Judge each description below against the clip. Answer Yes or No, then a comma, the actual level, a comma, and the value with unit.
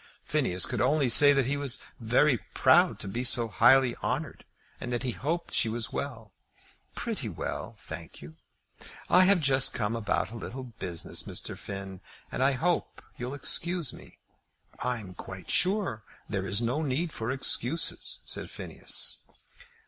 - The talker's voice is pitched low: Yes, low, 125 Hz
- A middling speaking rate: Yes, average, 165 wpm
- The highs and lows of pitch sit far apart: No, average, 4.4 semitones